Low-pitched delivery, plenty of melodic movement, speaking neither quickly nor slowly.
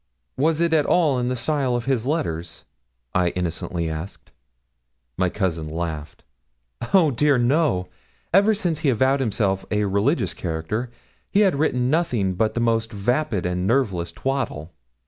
Yes: low, 115 Hz; wide, 7.8 semitones; average, 150 wpm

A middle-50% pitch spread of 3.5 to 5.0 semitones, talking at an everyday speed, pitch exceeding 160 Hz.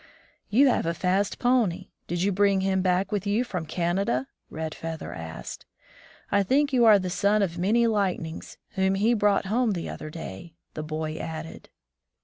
Yes: average, 4.1 semitones; average, 175 wpm; high, 190 Hz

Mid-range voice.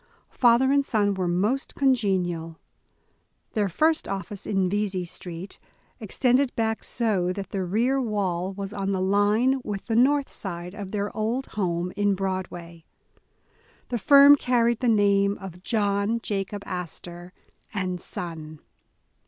No: high, 200 Hz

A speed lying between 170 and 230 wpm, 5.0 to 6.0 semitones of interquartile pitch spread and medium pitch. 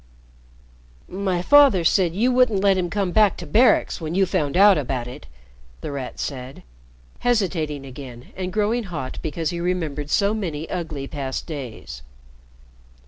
No: average, 150 wpm; wide, 5.6 semitones; medium, 175 Hz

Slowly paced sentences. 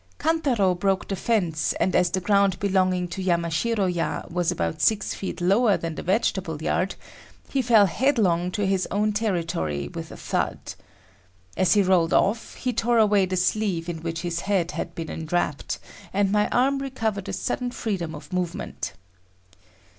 No: average, 170 wpm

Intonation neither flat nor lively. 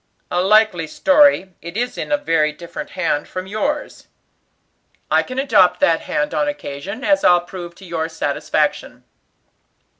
No: wide, 7.9 semitones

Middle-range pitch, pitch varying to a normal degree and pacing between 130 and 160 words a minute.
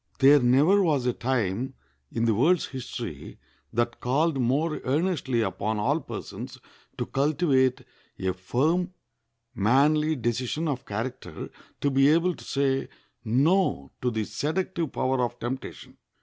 No: low, 130 Hz; average, 4.4 semitones; slow, 135 wpm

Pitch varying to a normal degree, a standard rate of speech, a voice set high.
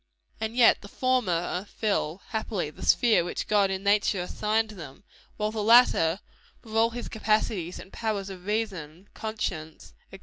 Yes: average, 3.5 semitones; average, 160 wpm; high, 210 Hz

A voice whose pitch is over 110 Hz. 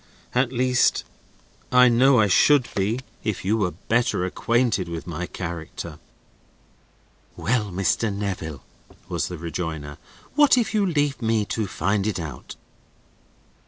No: low, 105 Hz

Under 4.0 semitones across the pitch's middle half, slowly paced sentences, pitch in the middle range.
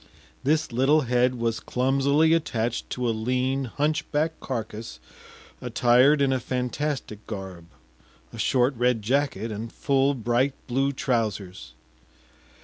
No: average, 3.4 semitones; slow, 125 wpm; low, 125 Hz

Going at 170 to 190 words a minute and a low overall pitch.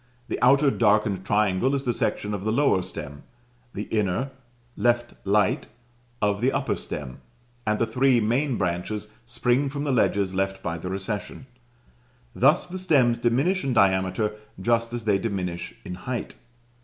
No: average, 155 wpm; low, 110 Hz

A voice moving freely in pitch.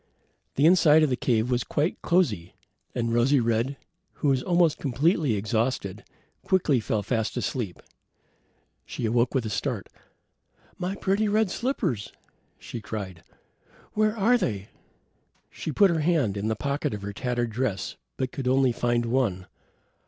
Yes: wide, 6.3 semitones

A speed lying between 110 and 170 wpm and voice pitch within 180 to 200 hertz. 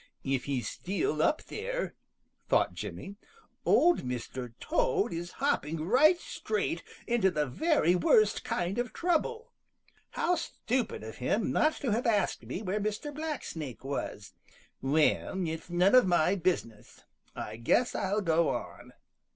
Yes: average, 140 wpm; high, 190 Hz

